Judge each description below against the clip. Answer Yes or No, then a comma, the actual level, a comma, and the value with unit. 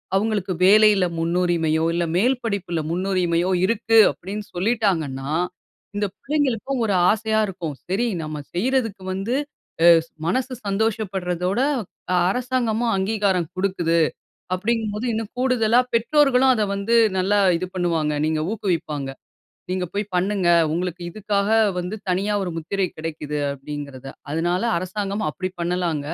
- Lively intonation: No, average, 4.1 semitones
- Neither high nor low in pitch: No, high, 195 Hz